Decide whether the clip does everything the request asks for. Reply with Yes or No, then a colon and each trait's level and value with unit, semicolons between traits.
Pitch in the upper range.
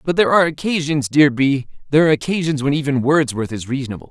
No: medium, 140 Hz